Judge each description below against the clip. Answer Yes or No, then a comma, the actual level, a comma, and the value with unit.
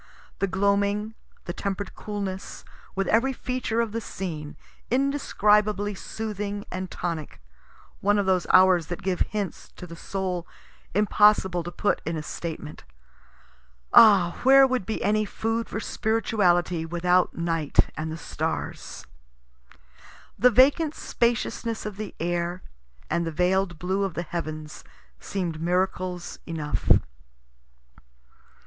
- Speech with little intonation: No, average, 3.5 semitones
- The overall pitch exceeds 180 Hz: Yes, high, 190 Hz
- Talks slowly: Yes, slow, 125 wpm